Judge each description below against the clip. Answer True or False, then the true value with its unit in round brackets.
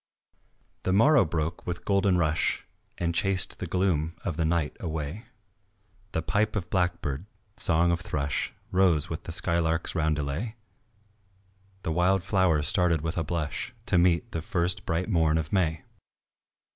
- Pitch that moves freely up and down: False (2.6 semitones)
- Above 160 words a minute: False (145 wpm)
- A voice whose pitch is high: False (85 Hz)